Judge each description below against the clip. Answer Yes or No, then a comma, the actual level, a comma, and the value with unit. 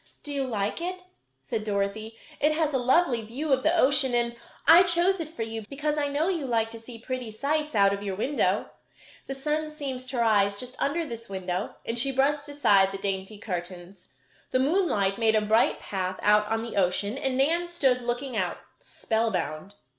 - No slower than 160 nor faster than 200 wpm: Yes, average, 195 wpm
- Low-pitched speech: No, high, 240 Hz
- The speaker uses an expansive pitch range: Yes, wide, 5.8 semitones